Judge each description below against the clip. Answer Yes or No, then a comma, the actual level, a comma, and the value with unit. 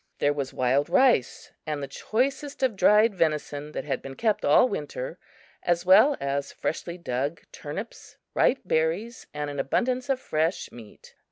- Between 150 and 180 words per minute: Yes, average, 160 wpm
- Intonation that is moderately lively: No, wide, 8.6 semitones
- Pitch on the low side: No, medium, 170 Hz